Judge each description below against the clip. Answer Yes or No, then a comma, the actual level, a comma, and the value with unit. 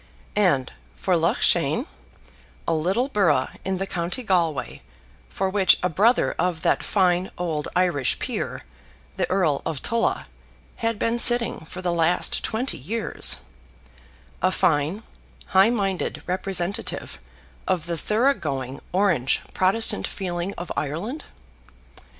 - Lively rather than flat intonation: No, average, 3.9 semitones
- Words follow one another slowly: Yes, slow, 125 wpm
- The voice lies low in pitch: No, medium, 180 Hz